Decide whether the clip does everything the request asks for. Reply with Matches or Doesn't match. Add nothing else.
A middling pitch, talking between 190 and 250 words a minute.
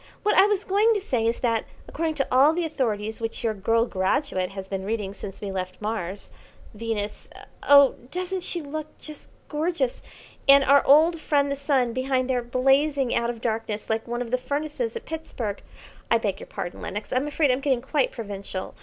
Doesn't match